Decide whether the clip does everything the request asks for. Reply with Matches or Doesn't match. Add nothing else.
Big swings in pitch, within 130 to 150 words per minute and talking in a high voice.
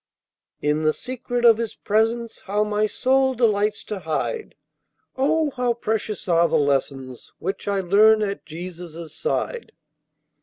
Matches